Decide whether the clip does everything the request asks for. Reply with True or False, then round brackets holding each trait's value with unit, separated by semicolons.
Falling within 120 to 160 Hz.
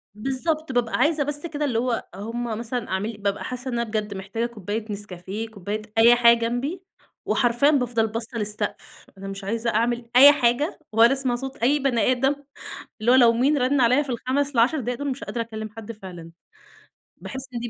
False (235 Hz)